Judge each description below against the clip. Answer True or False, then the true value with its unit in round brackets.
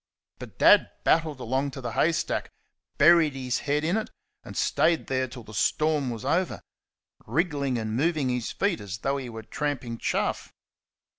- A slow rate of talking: False (165 wpm)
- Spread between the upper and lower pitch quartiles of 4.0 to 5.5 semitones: True (4.3 semitones)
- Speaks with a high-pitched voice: False (135 Hz)